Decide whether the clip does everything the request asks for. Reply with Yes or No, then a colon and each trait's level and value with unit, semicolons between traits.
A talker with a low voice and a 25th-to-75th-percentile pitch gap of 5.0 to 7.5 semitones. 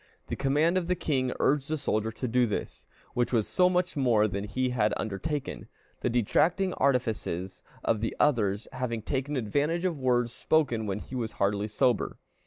Yes: low, 125 Hz; average, 5.3 semitones